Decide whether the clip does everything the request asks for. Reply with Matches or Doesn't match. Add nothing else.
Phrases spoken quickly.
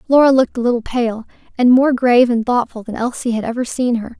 Matches